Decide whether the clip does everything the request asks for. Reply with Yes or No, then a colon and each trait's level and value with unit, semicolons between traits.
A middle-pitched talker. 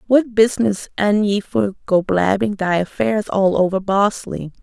No: high, 205 Hz